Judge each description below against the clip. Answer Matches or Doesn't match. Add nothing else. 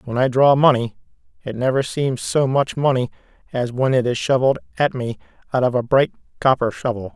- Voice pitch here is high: Doesn't match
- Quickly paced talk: Doesn't match